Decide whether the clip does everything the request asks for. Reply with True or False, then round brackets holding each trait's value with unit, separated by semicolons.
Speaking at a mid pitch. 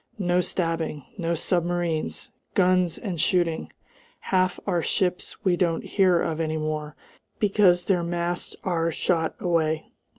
True (175 Hz)